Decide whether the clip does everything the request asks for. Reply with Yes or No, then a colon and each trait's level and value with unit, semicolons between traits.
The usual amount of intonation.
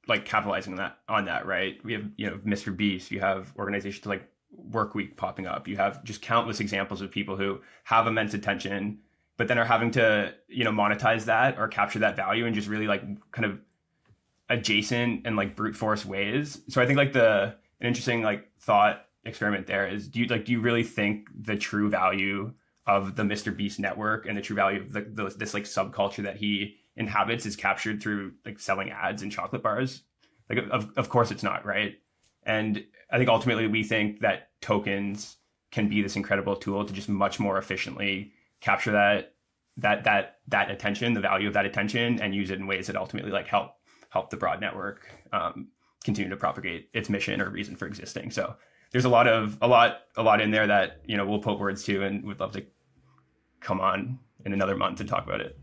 No: narrow, 2.0 semitones